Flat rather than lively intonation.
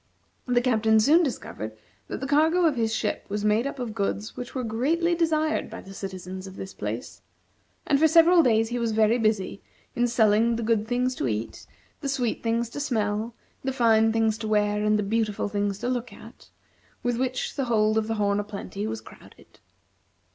No: average, 3.2 semitones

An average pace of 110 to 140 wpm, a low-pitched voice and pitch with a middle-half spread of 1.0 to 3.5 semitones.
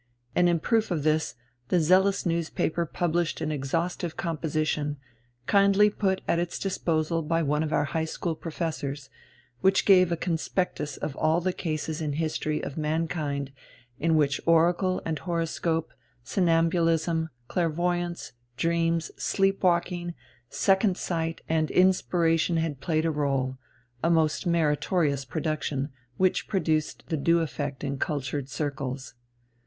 No: slow, 135 wpm; medium, 165 Hz; narrow, 2.4 semitones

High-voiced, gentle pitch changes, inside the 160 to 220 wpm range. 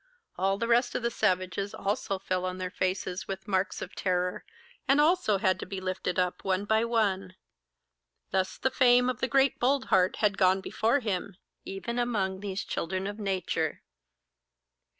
No: high, 195 Hz; average, 3.8 semitones; average, 170 wpm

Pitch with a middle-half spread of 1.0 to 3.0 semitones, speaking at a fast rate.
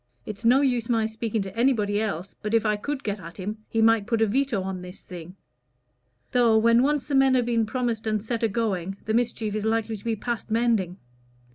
Yes: narrow, 2.4 semitones; fast, 225 wpm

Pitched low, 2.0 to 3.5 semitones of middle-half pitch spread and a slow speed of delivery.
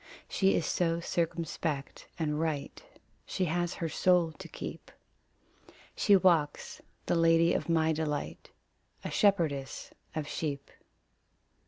No: medium, 165 Hz; narrow, 2.4 semitones; slow, 120 wpm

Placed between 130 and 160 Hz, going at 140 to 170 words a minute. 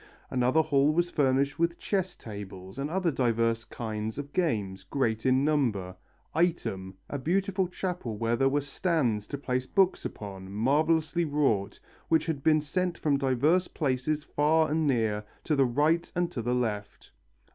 Yes: medium, 140 Hz; average, 160 wpm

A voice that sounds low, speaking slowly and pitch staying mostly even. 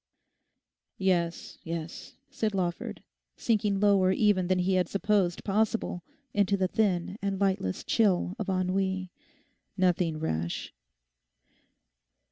No: high, 190 Hz; slow, 100 wpm; narrow, 2.2 semitones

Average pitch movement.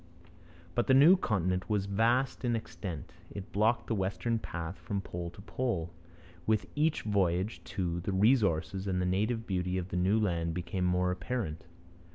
Yes: average, 3.8 semitones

